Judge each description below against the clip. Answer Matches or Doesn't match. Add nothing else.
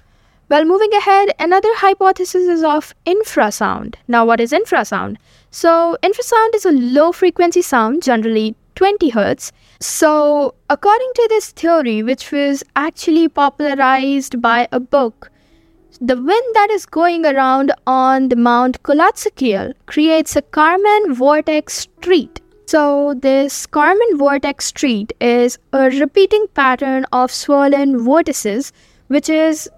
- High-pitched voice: Matches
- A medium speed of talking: Doesn't match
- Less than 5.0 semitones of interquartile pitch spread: Doesn't match